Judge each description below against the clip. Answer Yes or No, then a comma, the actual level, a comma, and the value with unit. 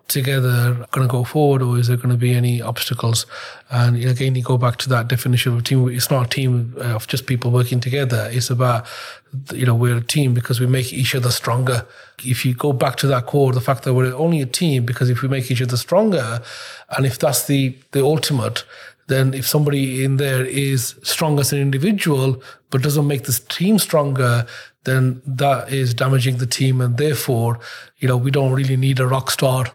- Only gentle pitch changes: Yes, narrow, 1.8 semitones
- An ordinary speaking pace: No, fast, 210 wpm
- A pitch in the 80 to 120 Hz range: No, low, 130 Hz